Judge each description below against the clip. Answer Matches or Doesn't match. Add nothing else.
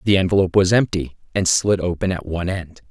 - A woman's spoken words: Doesn't match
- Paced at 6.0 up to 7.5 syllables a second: Matches